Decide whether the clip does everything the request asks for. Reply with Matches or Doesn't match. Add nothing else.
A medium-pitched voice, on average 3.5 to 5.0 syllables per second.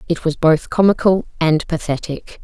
Matches